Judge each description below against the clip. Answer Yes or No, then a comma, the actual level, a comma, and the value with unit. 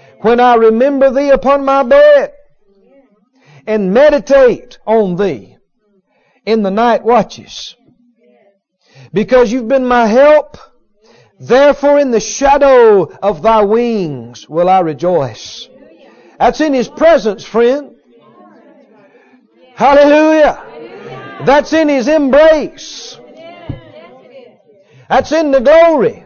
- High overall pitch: Yes, very high, 255 Hz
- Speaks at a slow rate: Yes, slow, 100 wpm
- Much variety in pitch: No, average, 5.0 semitones